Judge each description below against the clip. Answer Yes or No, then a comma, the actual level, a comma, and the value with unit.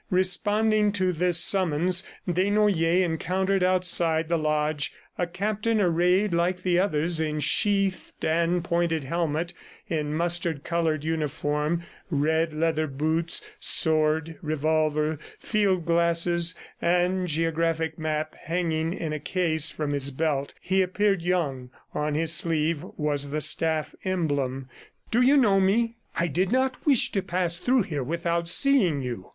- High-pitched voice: No, medium, 170 Hz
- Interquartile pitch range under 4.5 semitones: Yes, average, 3.0 semitones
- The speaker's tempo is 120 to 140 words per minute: Yes, slow, 135 wpm